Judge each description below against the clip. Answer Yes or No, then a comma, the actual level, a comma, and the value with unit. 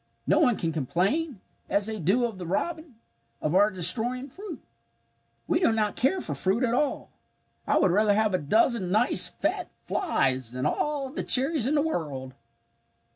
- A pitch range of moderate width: No, wide, 6.9 semitones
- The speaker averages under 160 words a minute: No, average, 175 wpm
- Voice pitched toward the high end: Yes, high, 220 Hz